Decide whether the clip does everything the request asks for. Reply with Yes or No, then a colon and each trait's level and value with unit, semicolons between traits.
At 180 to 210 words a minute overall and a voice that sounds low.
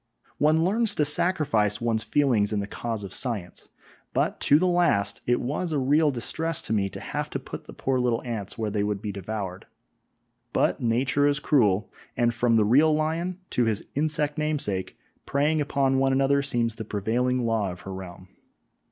Yes: average, 185 wpm; low, 125 Hz